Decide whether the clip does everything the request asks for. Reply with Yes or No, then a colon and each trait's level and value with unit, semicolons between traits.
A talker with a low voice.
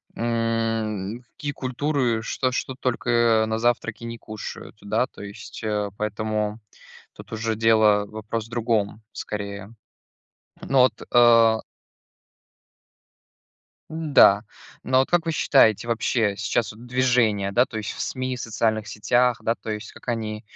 Yes: low, 115 Hz